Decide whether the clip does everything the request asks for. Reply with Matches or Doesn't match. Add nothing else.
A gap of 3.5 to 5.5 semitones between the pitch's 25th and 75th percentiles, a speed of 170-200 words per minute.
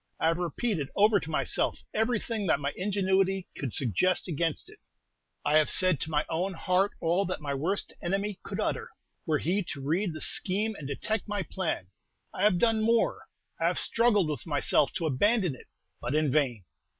Matches